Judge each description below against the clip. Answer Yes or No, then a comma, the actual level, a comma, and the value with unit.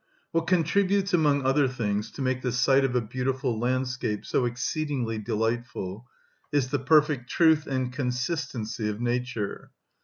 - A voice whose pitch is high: No, low, 130 Hz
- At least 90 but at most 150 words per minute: Yes, average, 145 wpm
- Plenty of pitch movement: No, average, 3.4 semitones